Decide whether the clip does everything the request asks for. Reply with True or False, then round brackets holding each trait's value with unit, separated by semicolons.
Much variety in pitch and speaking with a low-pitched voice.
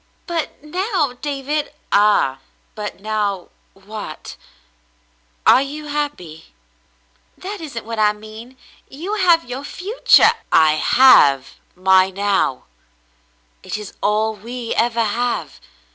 False (6.3 semitones; 230 Hz)